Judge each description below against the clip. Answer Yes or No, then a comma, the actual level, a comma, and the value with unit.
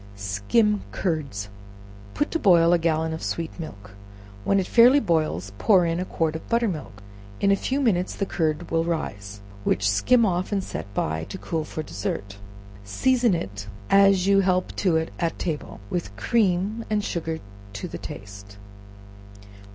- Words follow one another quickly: No, average, 165 wpm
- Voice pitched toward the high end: No, medium, 165 Hz